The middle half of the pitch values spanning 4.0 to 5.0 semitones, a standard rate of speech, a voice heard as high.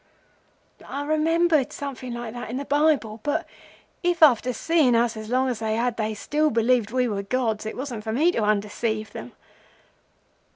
Yes: average, 4.7 semitones; average, 175 wpm; high, 245 Hz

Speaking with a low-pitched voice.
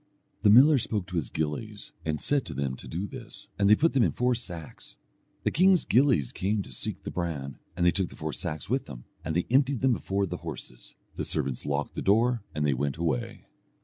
Yes: very low, 90 Hz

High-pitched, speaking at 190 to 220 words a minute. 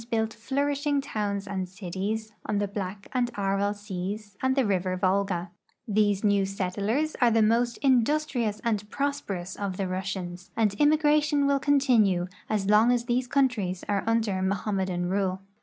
No: high, 210 Hz; average, 150 wpm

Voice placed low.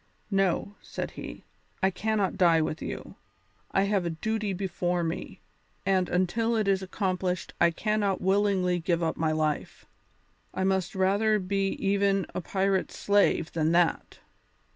No: high, 190 Hz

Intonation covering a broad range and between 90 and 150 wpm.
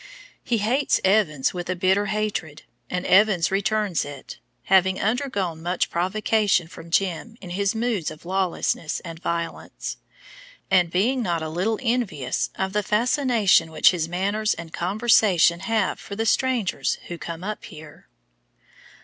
No: average, 4.0 semitones; average, 145 wpm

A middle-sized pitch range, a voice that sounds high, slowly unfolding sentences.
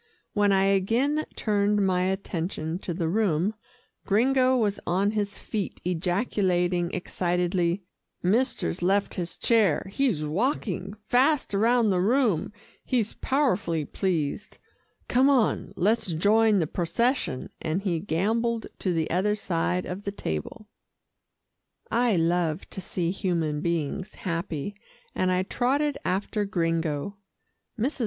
Yes: average, 4.2 semitones; high, 195 Hz; slow, 125 wpm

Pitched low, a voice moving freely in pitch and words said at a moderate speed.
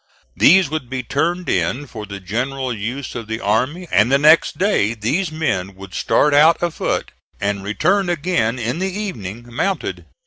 Yes: low, 130 Hz; wide, 7.6 semitones; average, 170 wpm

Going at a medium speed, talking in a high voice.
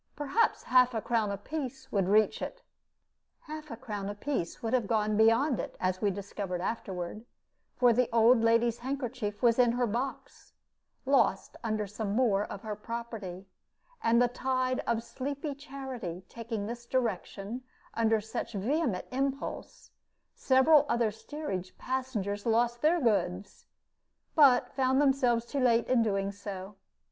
Yes: average, 145 wpm; high, 235 Hz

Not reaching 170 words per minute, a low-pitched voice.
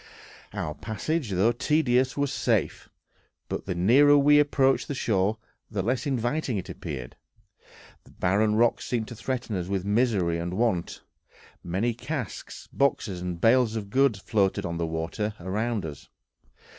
Yes: average, 150 wpm; low, 110 Hz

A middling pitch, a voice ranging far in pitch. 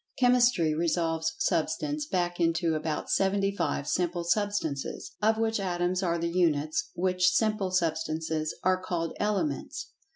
No: medium, 175 Hz; average, 3.5 semitones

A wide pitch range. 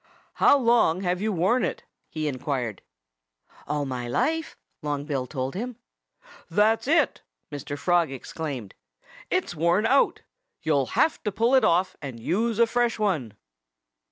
Yes: wide, 8.3 semitones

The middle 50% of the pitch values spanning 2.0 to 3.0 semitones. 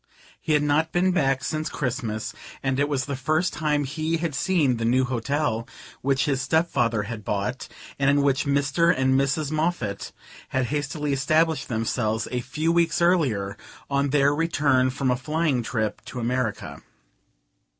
No: average, 3.7 semitones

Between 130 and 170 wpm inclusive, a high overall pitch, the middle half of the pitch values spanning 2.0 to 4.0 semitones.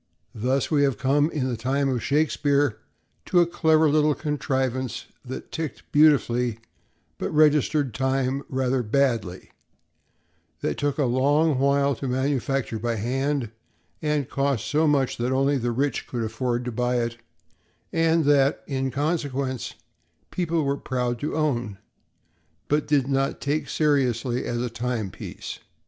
No: average, 140 wpm; low, 135 Hz; average, 2.9 semitones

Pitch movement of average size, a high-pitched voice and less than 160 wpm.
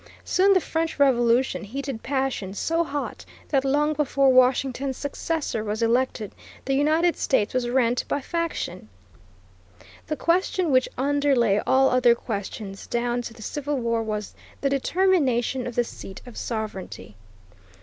Yes: average, 3.7 semitones; very high, 260 Hz; average, 140 wpm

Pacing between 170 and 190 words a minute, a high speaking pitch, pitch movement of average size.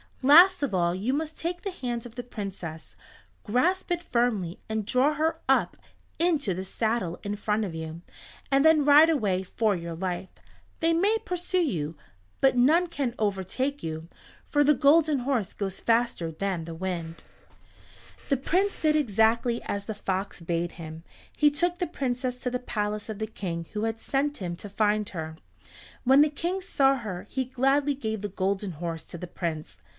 No: average, 180 wpm; high, 225 Hz; wide, 7.4 semitones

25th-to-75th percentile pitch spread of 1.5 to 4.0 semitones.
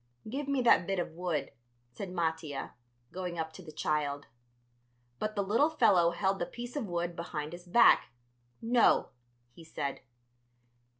No: average, 4.9 semitones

